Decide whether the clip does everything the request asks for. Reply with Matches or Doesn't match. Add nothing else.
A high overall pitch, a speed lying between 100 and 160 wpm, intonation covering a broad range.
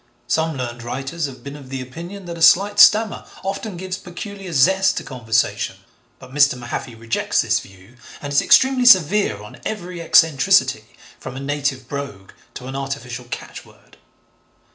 Doesn't match